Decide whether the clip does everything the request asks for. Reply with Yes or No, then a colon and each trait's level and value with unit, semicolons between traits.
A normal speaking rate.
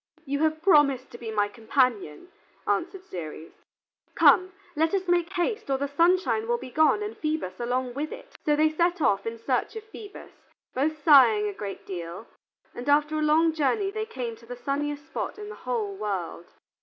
Yes: average, 190 wpm